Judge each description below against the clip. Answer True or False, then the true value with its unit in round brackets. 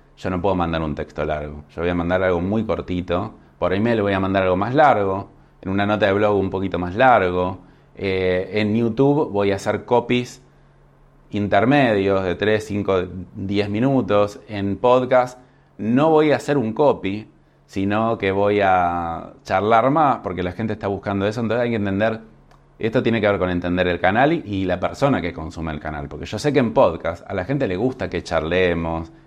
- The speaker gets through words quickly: True (200 wpm)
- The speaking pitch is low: True (100 Hz)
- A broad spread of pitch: False (3.8 semitones)